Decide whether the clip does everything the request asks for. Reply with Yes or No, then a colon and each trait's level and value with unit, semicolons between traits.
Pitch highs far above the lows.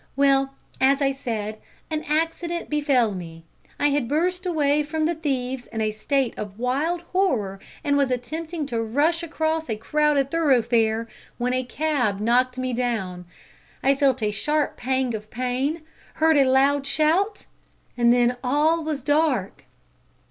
No: average, 4.2 semitones